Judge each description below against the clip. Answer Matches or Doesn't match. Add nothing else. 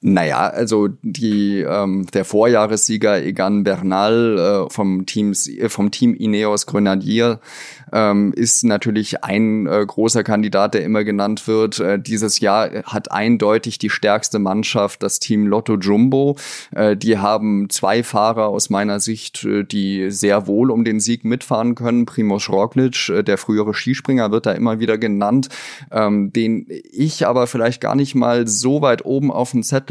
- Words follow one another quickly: Doesn't match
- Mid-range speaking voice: Doesn't match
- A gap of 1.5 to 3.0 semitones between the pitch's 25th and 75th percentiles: Matches